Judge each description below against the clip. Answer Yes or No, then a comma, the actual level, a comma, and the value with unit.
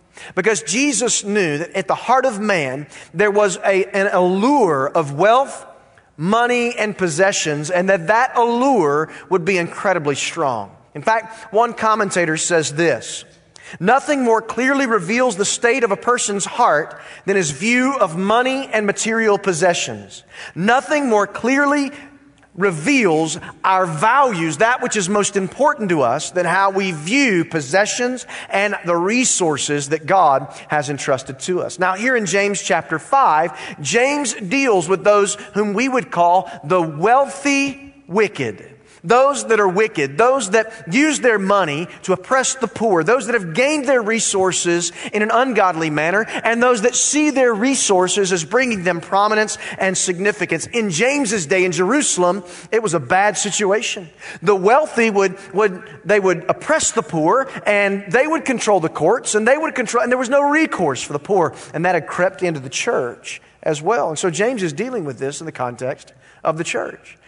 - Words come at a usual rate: Yes, average, 170 wpm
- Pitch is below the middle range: No, high, 205 Hz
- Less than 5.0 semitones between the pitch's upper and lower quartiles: No, wide, 5.4 semitones